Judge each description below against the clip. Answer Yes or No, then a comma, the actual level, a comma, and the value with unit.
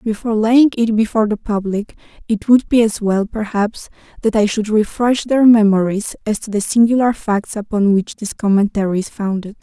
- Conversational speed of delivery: Yes, average, 180 wpm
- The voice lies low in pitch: No, high, 215 Hz